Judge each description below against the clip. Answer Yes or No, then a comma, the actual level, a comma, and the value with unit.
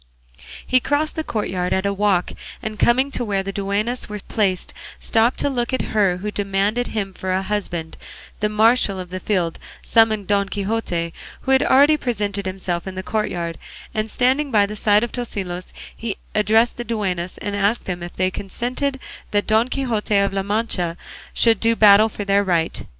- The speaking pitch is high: Yes, high, 205 Hz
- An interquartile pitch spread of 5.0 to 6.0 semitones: No, average, 3.2 semitones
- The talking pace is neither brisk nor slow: Yes, average, 185 wpm